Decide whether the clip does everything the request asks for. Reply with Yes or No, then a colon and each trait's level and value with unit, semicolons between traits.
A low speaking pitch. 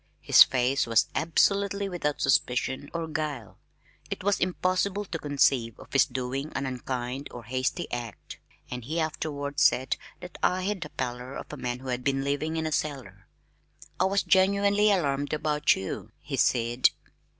No: medium, 145 Hz